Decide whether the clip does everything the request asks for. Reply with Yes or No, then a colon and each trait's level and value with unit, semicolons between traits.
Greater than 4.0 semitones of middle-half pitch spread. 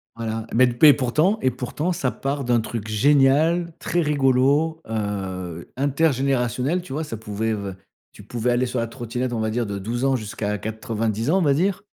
Yes: average, 4.5 semitones